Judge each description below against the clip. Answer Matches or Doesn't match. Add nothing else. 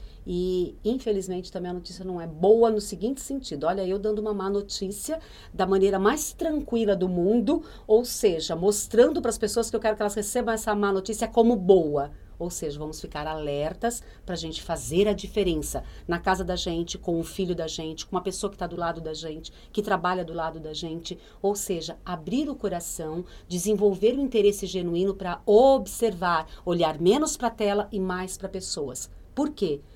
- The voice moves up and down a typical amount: Matches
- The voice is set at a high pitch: Matches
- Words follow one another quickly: Matches